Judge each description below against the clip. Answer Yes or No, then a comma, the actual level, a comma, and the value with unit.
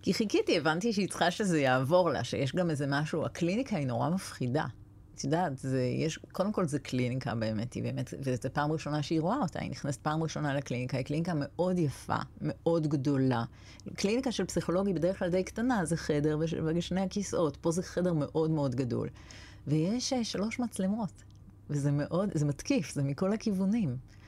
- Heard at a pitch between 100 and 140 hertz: No, medium, 155 Hz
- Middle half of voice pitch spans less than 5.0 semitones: No, wide, 5.6 semitones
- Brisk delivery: Yes, fast, 175 wpm